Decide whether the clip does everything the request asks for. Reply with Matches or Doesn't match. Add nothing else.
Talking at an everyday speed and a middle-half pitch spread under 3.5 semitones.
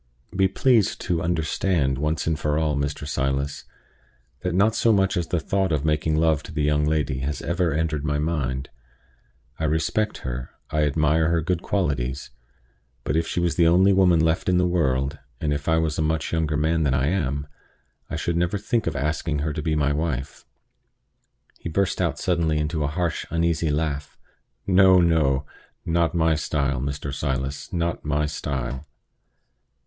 Matches